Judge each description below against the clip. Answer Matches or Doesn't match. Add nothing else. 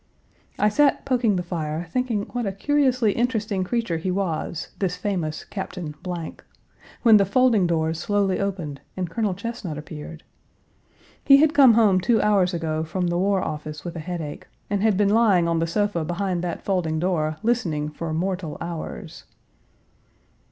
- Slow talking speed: Doesn't match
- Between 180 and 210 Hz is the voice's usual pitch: Matches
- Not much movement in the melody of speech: Doesn't match